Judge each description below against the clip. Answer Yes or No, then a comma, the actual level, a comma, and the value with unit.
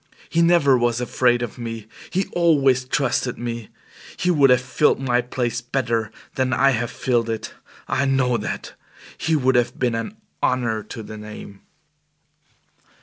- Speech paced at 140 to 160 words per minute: Yes, average, 155 wpm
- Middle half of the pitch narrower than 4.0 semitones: Yes, narrow, 2.4 semitones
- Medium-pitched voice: No, low, 125 Hz